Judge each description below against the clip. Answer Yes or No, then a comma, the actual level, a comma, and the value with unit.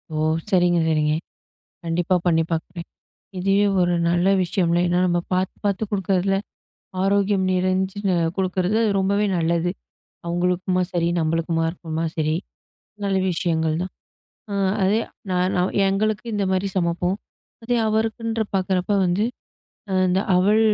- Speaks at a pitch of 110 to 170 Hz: No, medium, 185 Hz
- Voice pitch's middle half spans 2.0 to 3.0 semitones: Yes, narrow, 2.4 semitones